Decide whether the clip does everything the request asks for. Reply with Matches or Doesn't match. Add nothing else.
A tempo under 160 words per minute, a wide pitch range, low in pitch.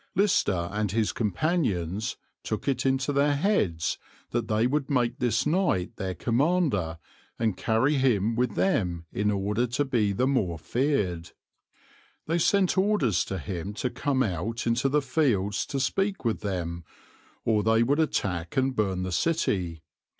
Matches